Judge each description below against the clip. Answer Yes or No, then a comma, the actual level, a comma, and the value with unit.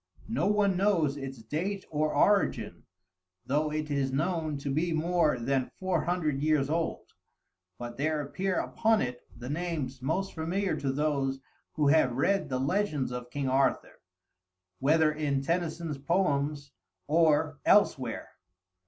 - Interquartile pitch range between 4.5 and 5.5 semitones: No, average, 4.0 semitones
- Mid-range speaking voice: Yes, medium, 150 Hz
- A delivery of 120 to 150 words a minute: Yes, average, 140 wpm